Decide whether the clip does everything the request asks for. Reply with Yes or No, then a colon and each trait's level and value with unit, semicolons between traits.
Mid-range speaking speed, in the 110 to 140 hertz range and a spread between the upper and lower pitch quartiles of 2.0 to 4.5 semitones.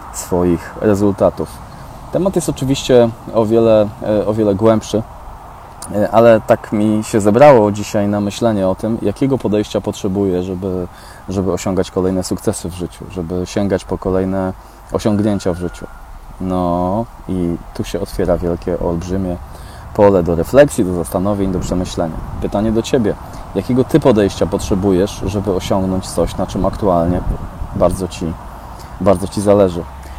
No: average, 135 wpm; very low, 95 Hz; average, 3.0 semitones